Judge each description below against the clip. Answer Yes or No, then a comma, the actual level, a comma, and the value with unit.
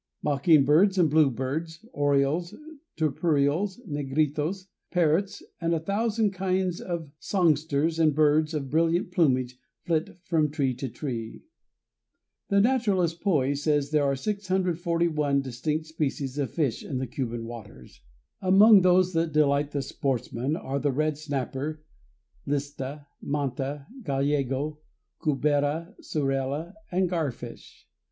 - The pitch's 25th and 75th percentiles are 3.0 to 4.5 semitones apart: Yes, average, 3.6 semitones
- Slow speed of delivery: Yes, slow, 120 wpm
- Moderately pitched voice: Yes, medium, 150 Hz